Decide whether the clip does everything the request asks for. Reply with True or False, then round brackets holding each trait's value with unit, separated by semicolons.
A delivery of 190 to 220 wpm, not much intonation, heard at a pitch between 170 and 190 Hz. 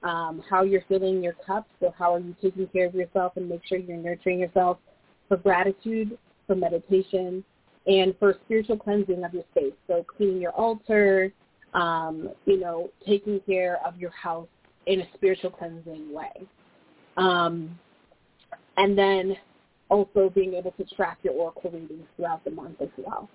False (165 wpm; 2.1 semitones; 185 Hz)